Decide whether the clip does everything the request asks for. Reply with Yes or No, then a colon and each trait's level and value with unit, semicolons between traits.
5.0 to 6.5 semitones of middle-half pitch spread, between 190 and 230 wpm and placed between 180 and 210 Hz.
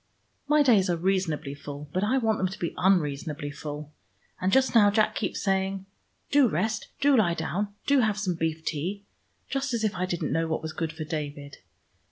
Yes: average, 5.3 semitones; average, 200 wpm; medium, 185 Hz